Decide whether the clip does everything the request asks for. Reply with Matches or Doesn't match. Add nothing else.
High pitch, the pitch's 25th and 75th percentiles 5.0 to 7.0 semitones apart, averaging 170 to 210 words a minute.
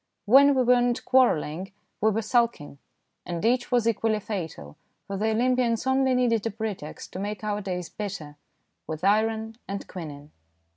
Doesn't match